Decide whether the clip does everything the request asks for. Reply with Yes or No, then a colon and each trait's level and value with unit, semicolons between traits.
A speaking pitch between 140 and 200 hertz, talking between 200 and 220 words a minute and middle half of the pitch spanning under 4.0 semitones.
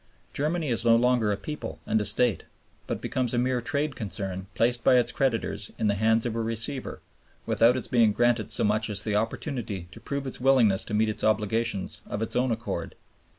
No: low, 115 Hz; fast, 205 wpm; average, 2.8 semitones